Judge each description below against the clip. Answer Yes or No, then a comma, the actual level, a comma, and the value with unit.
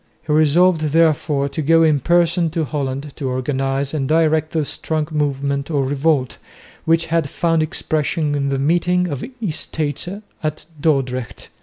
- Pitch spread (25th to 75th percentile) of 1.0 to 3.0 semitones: Yes, average, 2.7 semitones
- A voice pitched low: No, medium, 150 Hz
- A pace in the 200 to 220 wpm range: No, average, 155 wpm